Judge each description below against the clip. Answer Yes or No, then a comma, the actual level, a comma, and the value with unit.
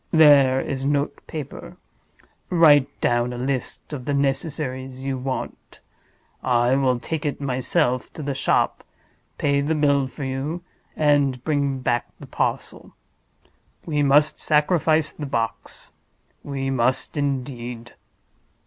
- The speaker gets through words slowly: Yes, slow, 120 wpm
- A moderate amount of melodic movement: No, narrow, 2.3 semitones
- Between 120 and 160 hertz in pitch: Yes, medium, 140 Hz